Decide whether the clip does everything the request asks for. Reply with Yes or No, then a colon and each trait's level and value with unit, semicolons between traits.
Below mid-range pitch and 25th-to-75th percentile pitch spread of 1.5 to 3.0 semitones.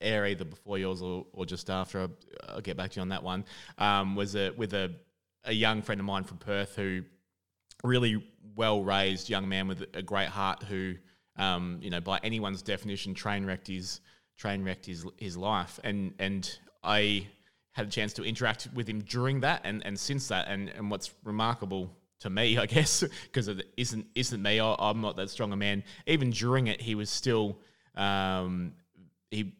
Yes: low, 100 Hz; narrow, 2.4 semitones